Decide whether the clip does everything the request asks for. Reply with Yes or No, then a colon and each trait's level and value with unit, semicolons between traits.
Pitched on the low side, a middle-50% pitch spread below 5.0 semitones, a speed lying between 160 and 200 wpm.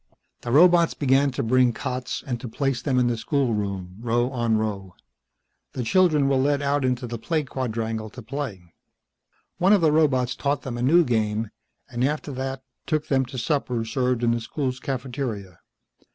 Yes: low, 125 Hz; average, 3.4 semitones; average, 180 wpm